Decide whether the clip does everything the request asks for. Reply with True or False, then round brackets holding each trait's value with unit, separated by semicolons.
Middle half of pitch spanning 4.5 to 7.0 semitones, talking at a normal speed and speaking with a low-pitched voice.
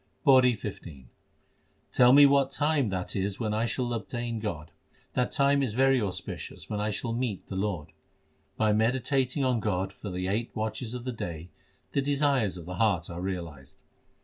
True (5.1 semitones; 175 wpm; 110 Hz)